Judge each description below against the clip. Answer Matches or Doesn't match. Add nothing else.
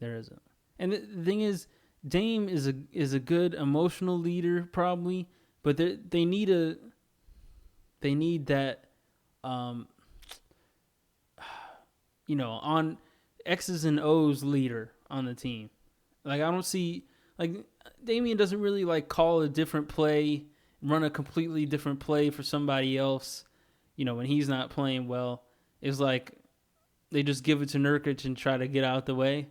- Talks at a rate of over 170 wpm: Doesn't match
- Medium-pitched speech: Matches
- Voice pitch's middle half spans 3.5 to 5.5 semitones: Matches